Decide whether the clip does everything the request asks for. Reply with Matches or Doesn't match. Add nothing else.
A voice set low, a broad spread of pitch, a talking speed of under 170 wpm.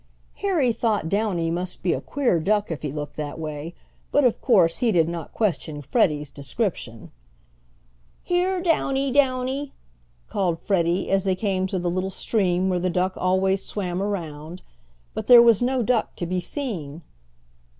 Doesn't match